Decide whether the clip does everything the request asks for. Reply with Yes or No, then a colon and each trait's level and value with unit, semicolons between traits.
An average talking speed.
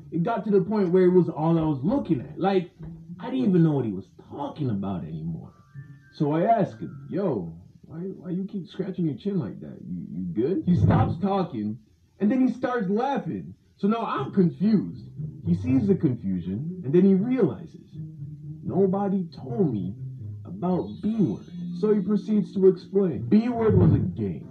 Yes: average, 190 wpm